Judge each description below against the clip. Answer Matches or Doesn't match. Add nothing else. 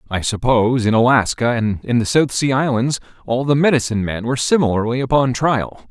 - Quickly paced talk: Doesn't match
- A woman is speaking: Doesn't match